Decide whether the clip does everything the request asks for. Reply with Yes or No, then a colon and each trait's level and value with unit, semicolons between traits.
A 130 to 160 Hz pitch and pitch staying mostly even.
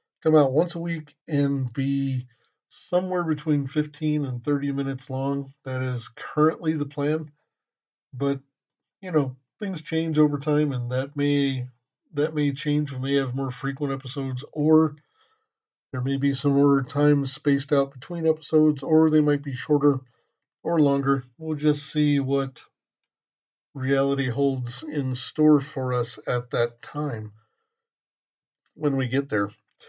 Yes: medium, 140 Hz; narrow, 2.2 semitones